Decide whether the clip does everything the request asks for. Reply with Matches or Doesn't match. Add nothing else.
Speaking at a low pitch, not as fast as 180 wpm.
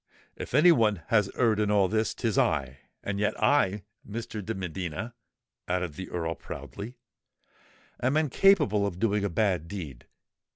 Matches